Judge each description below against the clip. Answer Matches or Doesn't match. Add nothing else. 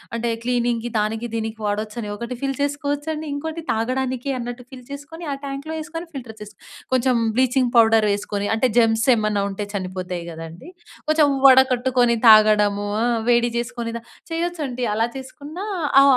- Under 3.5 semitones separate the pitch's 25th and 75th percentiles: Doesn't match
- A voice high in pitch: Matches